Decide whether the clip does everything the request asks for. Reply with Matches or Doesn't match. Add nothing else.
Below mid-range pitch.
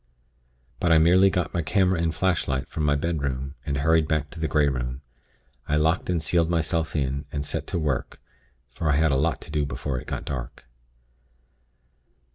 Matches